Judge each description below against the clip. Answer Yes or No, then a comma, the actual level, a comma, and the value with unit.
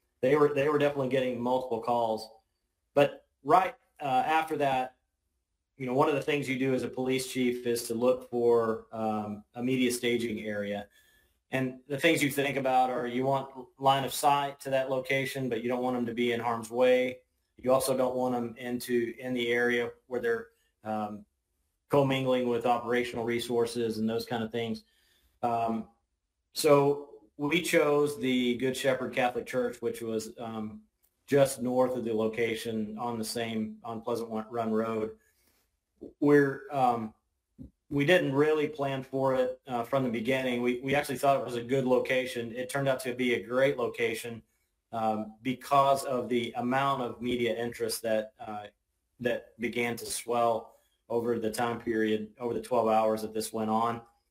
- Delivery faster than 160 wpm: Yes, average, 175 wpm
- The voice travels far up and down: No, average, 2.8 semitones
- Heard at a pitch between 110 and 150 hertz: Yes, low, 120 Hz